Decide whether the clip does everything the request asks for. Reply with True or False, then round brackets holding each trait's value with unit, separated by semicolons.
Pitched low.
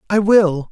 False (190 Hz)